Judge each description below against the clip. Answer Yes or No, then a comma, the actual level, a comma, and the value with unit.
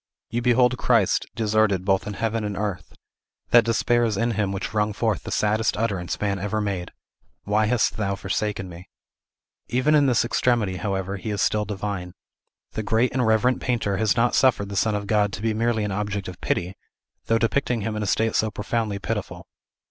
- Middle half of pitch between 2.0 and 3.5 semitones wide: Yes, narrow, 2.4 semitones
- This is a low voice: Yes, low, 105 Hz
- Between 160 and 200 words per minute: Yes, average, 195 wpm